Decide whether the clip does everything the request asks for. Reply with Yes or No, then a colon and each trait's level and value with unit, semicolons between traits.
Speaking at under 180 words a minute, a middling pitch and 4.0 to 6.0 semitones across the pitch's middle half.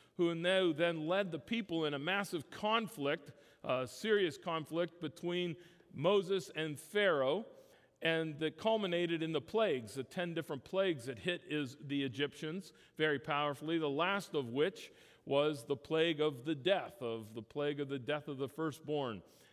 No: average, 165 wpm; medium, 160 Hz; average, 3.6 semitones